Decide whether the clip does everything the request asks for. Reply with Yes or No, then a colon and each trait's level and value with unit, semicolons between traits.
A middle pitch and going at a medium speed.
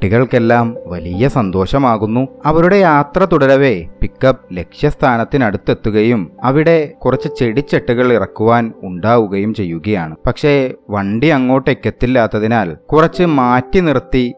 No: low, 125 Hz; average, 85 wpm